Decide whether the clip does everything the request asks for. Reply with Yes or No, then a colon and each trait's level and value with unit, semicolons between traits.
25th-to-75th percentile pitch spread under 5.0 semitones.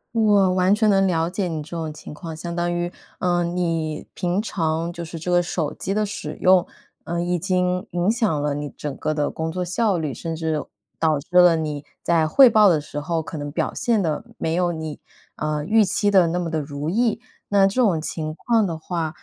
Yes: average, 3.1 semitones